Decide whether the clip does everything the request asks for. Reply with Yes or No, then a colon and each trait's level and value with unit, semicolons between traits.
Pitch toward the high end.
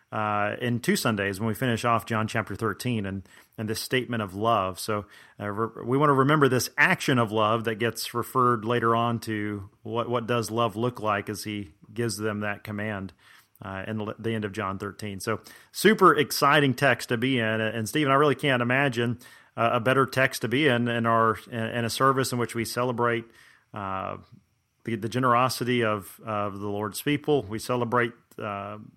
No: low, 115 Hz